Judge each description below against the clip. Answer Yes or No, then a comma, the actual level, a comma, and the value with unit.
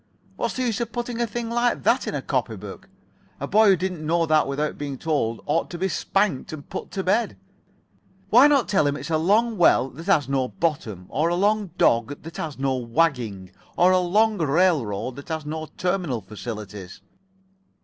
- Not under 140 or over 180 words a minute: No, average, 200 wpm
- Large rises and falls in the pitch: Yes, wide, 6.2 semitones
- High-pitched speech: No, medium, 160 Hz